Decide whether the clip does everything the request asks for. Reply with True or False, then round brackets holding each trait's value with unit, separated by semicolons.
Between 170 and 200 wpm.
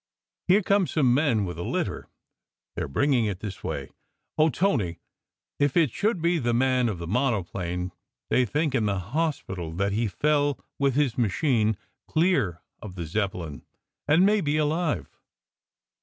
False (160 wpm)